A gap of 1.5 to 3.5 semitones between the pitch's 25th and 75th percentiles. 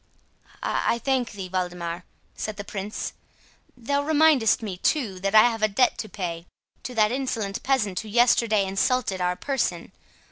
No: average, 4.7 semitones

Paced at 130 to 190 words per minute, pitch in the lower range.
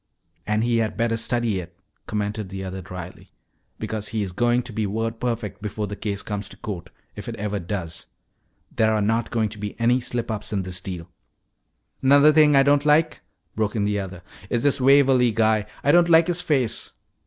No: average, 200 wpm; low, 110 Hz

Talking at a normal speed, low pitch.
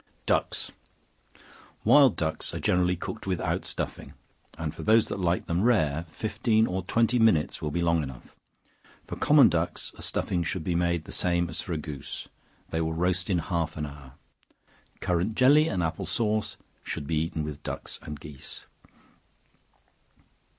Yes: average, 165 wpm; very low, 85 Hz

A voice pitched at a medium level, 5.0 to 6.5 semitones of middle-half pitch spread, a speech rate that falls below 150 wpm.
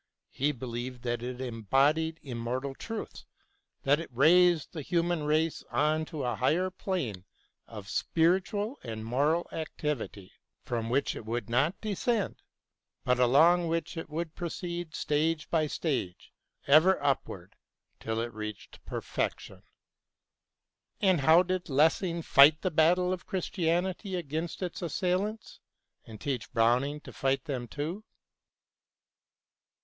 Yes: medium, 155 Hz; wide, 5.5 semitones; slow, 135 wpm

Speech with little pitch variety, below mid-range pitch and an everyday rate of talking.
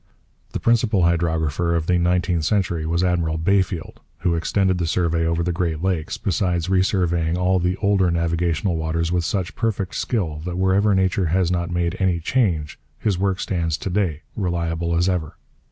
Yes: narrow, 2.1 semitones; very low, 85 Hz; average, 175 wpm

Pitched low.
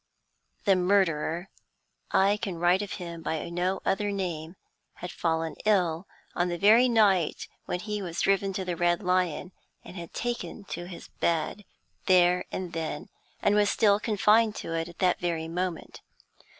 No: medium, 180 Hz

